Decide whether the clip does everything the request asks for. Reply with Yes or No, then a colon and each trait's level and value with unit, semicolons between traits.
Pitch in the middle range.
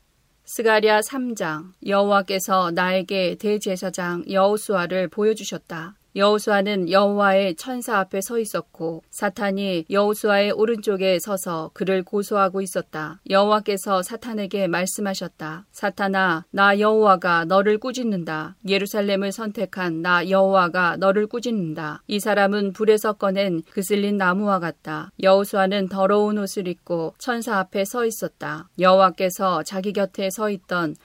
No: high, 195 Hz